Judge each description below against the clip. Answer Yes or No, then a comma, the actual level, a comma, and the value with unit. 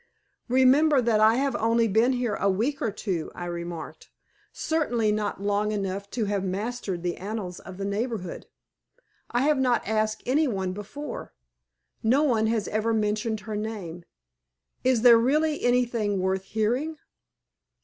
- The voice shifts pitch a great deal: No, average, 3.6 semitones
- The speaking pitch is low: No, high, 220 Hz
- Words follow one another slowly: No, average, 150 wpm